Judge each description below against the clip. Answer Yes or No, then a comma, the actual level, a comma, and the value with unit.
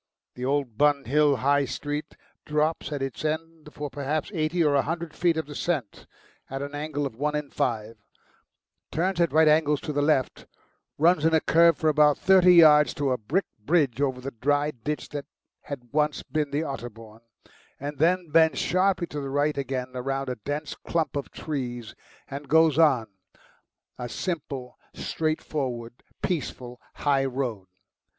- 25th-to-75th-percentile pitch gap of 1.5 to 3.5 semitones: Yes, average, 2.8 semitones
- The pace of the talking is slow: No, average, 165 wpm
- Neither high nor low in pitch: Yes, medium, 145 Hz